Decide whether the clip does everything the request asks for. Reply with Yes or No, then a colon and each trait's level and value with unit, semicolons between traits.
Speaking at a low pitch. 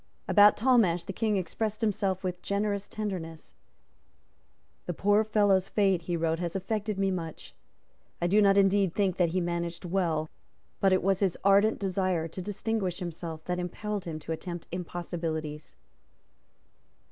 No: medium, 185 Hz